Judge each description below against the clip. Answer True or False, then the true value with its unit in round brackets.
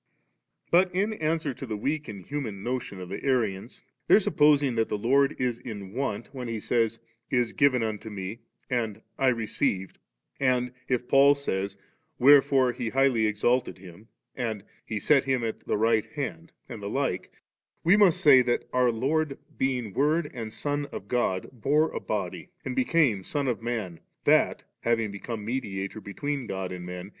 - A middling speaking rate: True (180 wpm)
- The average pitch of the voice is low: True (120 Hz)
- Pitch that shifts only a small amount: False (4.8 semitones)